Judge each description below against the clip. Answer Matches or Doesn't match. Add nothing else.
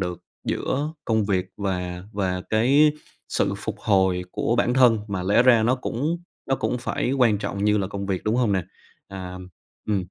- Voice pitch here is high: Doesn't match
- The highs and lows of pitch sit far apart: Doesn't match